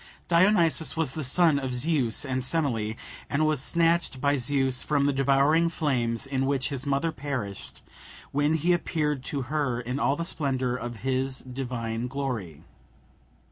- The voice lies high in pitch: No, low, 135 Hz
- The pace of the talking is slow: No, average, 155 wpm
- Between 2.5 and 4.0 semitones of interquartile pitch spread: Yes, average, 3.3 semitones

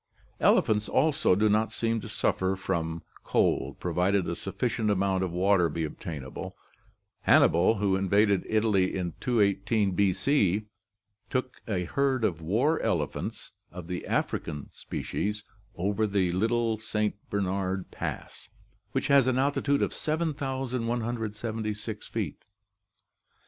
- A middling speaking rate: No, slow, 120 wpm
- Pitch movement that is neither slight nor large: Yes, average, 3.8 semitones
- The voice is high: No, low, 105 Hz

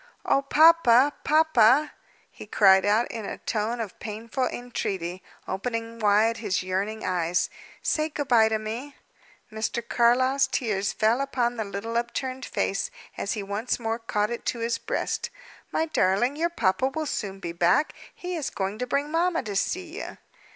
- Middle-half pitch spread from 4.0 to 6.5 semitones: Yes, average, 4.5 semitones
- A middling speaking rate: Yes, average, 165 wpm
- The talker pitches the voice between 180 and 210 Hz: No, high, 230 Hz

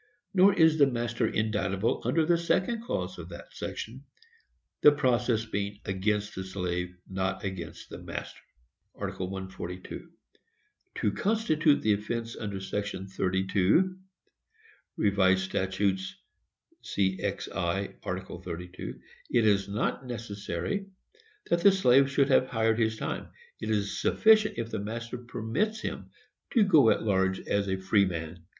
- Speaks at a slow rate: Yes, slow, 130 wpm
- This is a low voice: Yes, low, 105 Hz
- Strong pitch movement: Yes, wide, 6.0 semitones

